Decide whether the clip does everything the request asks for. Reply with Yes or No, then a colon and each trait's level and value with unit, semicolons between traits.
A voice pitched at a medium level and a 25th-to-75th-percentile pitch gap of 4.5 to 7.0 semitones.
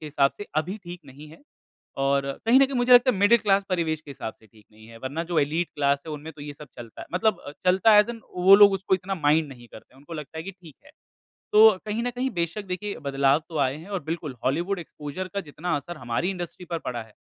Yes: medium, 165 Hz; wide, 5.5 semitones